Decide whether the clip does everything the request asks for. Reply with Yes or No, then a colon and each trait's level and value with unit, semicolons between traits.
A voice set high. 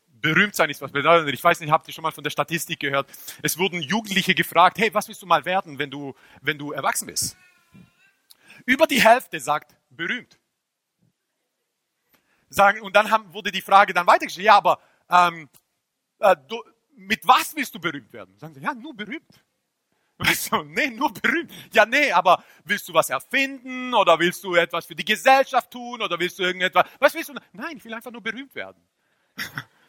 Yes: high, 195 Hz